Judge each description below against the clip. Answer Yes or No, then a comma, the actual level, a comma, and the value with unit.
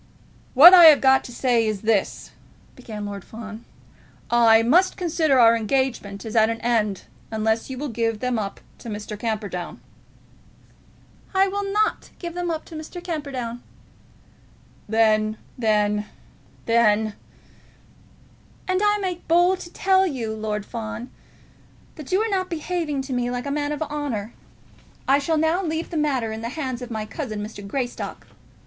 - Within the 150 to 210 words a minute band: Yes, average, 160 wpm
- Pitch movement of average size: No, wide, 6.5 semitones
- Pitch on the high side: Yes, high, 245 Hz